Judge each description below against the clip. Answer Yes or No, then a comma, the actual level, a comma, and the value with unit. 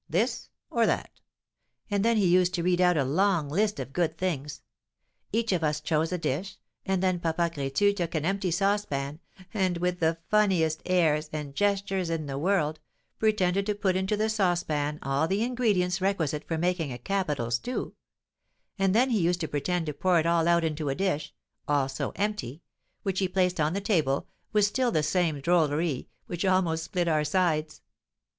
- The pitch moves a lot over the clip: No, average, 4.1 semitones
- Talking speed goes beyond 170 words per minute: Yes, average, 185 wpm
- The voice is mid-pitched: Yes, medium, 175 Hz